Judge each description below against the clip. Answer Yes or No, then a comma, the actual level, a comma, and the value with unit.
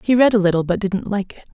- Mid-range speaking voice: No, high, 200 Hz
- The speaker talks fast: Yes, fast, 310 wpm